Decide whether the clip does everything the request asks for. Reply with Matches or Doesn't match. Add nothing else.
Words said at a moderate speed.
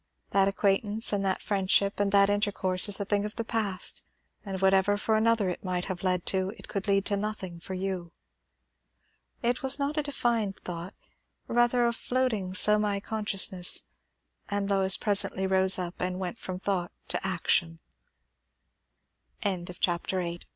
Matches